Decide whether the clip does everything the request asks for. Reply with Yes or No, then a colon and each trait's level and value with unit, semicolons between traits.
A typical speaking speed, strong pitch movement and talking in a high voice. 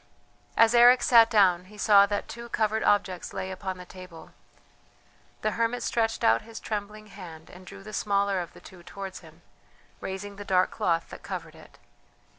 No: average, 180 wpm; average, 2.8 semitones; high, 200 Hz